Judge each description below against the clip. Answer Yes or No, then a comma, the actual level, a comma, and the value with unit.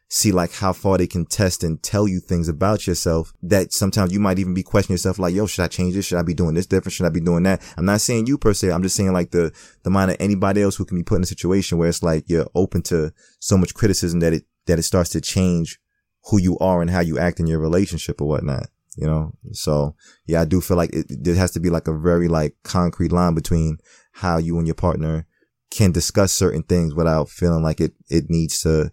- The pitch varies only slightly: Yes, narrow, 2.3 semitones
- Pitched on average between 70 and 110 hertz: Yes, very low, 90 Hz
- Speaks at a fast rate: Yes, fast, 260 wpm